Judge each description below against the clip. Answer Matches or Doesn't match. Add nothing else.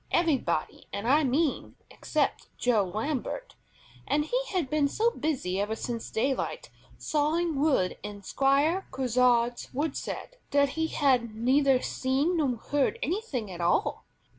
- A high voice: Matches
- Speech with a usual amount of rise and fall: Matches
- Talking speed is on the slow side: Matches